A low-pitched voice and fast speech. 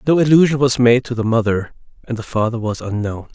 Yes: low, 120 Hz; fast, 215 wpm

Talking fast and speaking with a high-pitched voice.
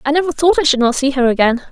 Yes: fast, 315 wpm; very high, 280 Hz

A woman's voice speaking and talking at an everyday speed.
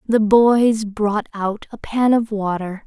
Yes: female; average, 165 wpm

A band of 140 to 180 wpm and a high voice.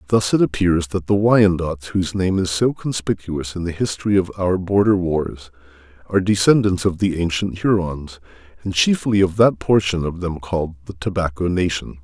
No: average, 175 wpm; very low, 90 Hz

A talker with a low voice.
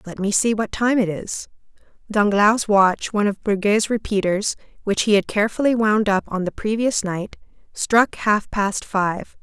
No: high, 210 Hz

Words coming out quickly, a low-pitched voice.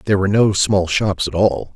Yes: fast, 240 wpm; very low, 95 Hz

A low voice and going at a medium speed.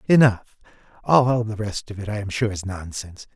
Yes: low, 105 Hz; average, 195 wpm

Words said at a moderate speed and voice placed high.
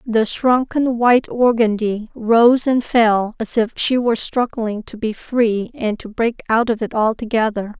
Yes: average, 170 wpm; high, 230 Hz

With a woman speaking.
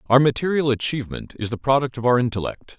No: male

